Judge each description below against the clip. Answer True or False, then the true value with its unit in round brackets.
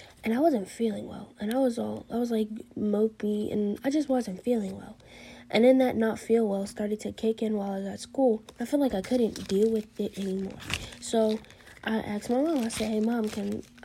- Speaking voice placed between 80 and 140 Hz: False (220 Hz)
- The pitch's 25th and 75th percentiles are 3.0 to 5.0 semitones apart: False (2.5 semitones)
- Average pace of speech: False (230 wpm)